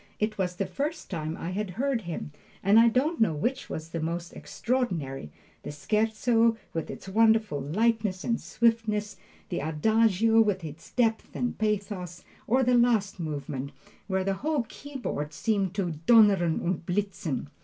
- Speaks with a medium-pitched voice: No, high, 205 Hz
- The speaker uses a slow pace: No, average, 155 wpm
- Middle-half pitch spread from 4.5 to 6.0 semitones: Yes, average, 5.1 semitones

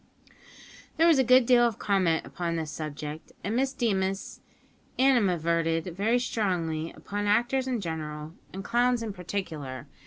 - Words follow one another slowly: No, average, 145 wpm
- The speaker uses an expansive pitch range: Yes, wide, 6.7 semitones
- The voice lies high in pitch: Yes, high, 195 Hz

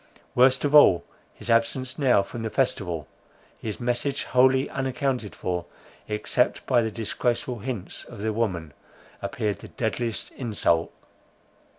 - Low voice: Yes, low, 115 Hz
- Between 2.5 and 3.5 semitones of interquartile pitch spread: No, average, 3.9 semitones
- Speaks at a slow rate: Yes, slow, 130 wpm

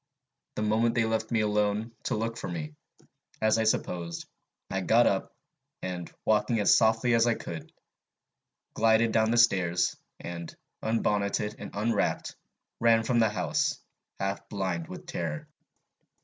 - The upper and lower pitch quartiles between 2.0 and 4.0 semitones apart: Yes, average, 3.3 semitones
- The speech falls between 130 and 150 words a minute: Yes, average, 145 wpm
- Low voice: Yes, low, 105 Hz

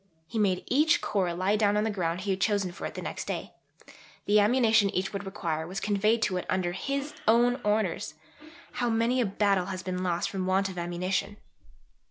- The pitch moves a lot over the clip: No, average, 3.0 semitones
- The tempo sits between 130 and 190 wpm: No, fast, 205 wpm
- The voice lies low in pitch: No, high, 200 Hz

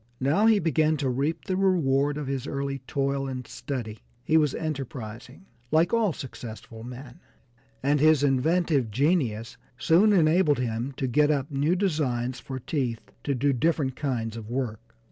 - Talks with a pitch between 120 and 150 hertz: Yes, medium, 140 Hz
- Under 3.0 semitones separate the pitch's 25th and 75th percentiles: No, average, 3.8 semitones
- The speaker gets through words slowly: No, average, 160 wpm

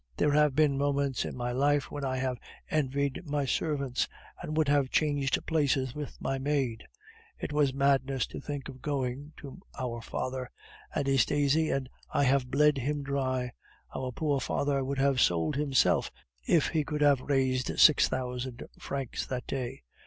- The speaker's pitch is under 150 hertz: Yes, medium, 140 Hz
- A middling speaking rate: Yes, average, 165 wpm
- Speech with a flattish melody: Yes, narrow, 1.9 semitones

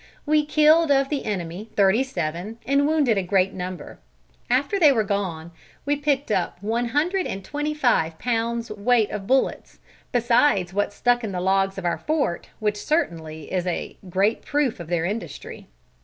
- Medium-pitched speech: No, high, 220 Hz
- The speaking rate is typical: Yes, average, 170 wpm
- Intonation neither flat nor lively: No, wide, 6.8 semitones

